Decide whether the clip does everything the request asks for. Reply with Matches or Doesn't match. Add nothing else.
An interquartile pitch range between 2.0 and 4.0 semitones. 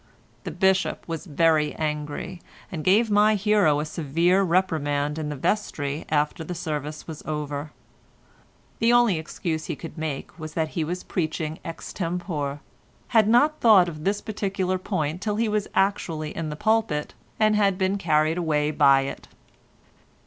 Doesn't match